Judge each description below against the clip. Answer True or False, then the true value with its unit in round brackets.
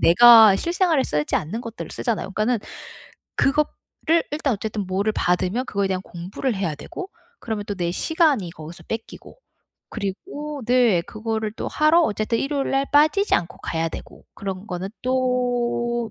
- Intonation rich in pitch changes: True (6.0 semitones)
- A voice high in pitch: True (225 Hz)